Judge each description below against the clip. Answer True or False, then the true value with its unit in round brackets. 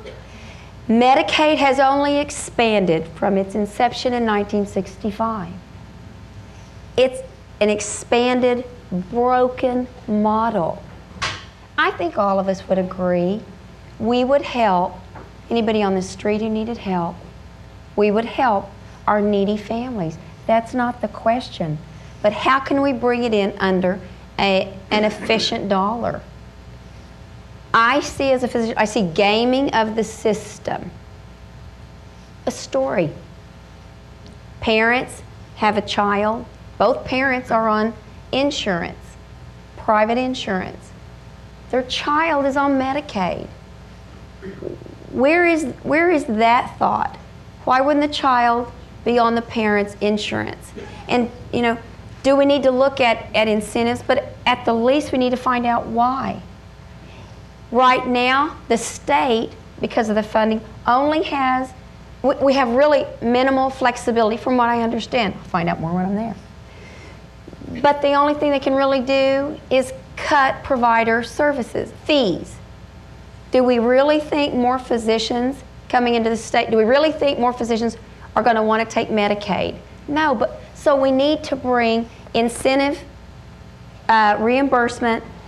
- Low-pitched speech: False (235 Hz)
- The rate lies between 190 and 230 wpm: False (135 wpm)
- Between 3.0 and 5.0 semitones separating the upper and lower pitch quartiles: True (3.7 semitones)